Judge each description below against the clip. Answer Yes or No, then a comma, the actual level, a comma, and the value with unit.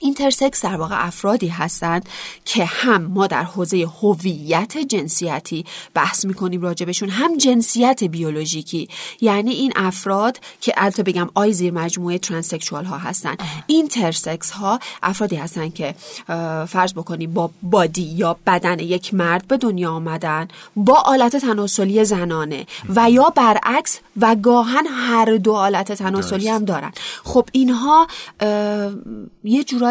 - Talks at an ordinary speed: Yes, average, 130 wpm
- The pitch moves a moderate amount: Yes, average, 5.0 semitones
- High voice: Yes, high, 195 Hz